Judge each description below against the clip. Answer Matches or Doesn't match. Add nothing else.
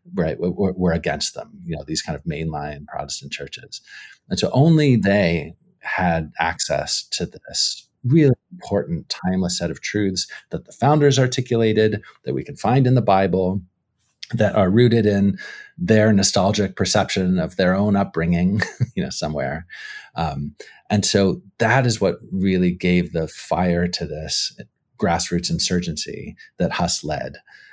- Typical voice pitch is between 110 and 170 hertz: Doesn't match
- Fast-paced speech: Doesn't match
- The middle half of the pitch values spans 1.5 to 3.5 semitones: Doesn't match